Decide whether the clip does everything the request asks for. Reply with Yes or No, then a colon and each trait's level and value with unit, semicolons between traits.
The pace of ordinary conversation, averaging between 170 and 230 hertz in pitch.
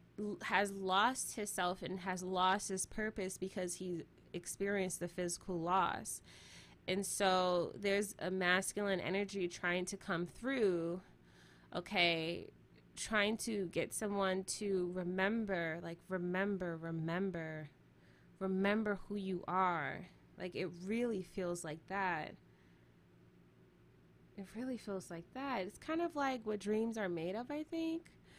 No: slow, 125 wpm; medium, 185 Hz